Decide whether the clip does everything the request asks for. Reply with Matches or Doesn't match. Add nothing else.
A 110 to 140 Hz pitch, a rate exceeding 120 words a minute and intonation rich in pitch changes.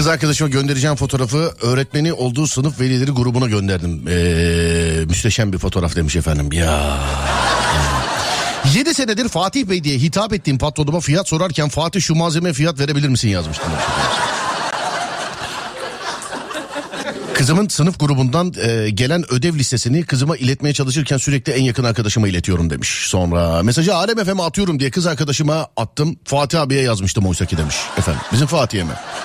Matches